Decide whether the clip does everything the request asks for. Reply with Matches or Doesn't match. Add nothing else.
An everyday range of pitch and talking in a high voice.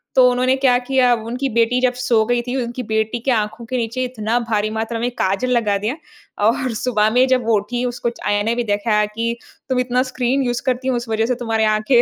Doesn't match